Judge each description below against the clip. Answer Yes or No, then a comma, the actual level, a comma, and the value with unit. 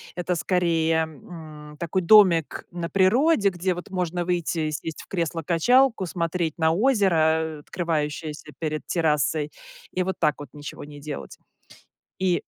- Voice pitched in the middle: Yes, medium, 170 Hz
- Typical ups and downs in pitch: Yes, average, 3.0 semitones